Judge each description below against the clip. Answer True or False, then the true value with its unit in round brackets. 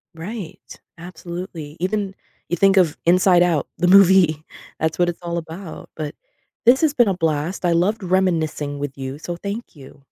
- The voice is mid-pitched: True (175 Hz)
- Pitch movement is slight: False (3.2 semitones)